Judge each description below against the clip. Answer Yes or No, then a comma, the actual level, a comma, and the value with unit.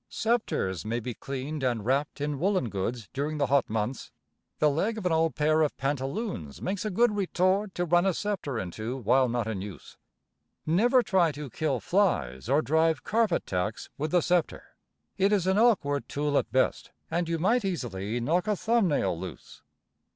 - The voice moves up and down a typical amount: No, wide, 7.5 semitones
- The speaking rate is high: No, average, 185 wpm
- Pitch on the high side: No, medium, 150 Hz